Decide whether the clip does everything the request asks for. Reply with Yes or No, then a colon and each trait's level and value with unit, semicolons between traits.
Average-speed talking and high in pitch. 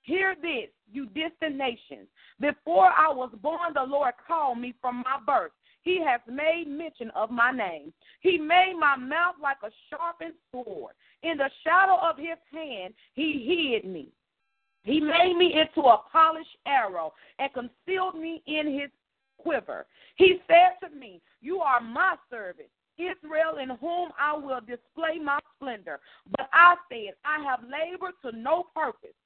Yes: average, 160 wpm; very high, 310 Hz